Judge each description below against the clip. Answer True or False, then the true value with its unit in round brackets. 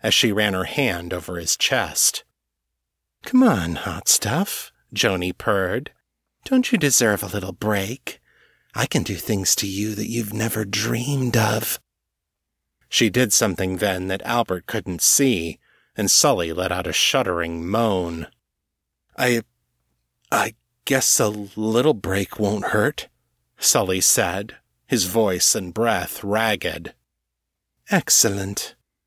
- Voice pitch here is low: True (100 Hz)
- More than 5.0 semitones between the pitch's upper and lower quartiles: True (5.5 semitones)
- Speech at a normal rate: False (130 wpm)